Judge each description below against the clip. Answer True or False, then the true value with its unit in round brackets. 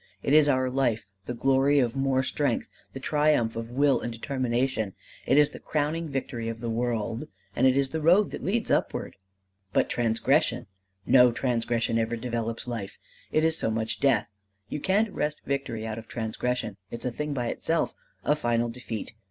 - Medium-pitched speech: False (125 Hz)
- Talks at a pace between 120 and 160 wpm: False (180 wpm)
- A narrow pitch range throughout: False (3.7 semitones)